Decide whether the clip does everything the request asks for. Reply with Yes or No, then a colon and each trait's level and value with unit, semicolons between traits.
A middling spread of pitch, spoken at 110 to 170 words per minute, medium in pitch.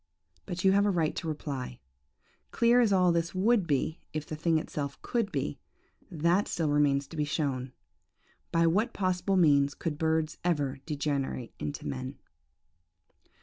Yes: average, 4.1 semitones; average, 155 wpm; medium, 160 Hz